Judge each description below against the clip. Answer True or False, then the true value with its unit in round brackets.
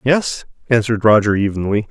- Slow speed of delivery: True (125 wpm)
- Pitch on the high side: False (110 Hz)